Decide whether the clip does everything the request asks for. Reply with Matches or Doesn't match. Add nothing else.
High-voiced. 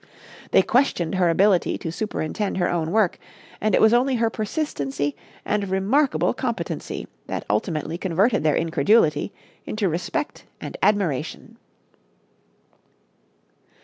Matches